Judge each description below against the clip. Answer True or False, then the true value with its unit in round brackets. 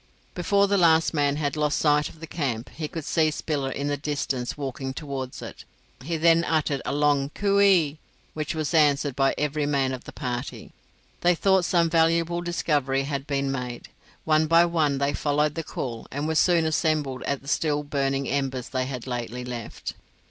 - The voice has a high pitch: False (145 Hz)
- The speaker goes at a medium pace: True (190 wpm)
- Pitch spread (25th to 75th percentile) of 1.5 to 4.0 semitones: True (3.0 semitones)